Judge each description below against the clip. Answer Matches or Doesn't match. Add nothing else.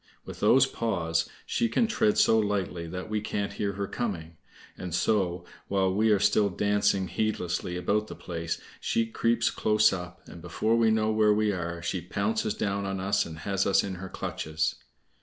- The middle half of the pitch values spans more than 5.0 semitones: Doesn't match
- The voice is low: Matches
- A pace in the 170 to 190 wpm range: Matches